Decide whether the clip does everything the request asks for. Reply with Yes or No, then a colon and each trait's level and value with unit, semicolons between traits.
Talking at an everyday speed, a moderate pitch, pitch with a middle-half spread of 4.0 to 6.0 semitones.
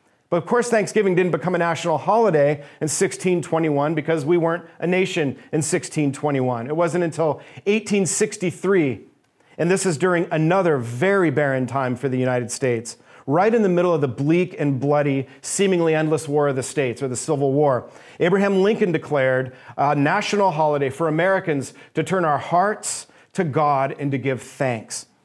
Yes: average, 165 wpm; medium, 160 Hz; average, 4.4 semitones